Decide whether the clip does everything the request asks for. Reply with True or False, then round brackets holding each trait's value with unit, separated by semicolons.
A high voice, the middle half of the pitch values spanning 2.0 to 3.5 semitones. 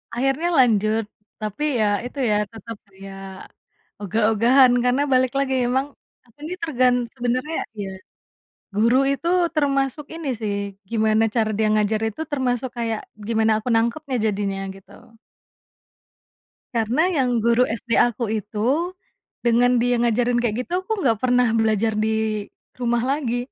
True (235 Hz; 2.9 semitones)